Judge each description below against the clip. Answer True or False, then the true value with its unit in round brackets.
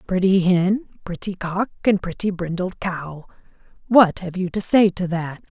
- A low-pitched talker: False (185 Hz)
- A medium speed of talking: True (160 wpm)